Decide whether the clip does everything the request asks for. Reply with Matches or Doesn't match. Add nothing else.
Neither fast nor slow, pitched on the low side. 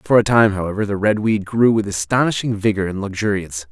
Doesn't match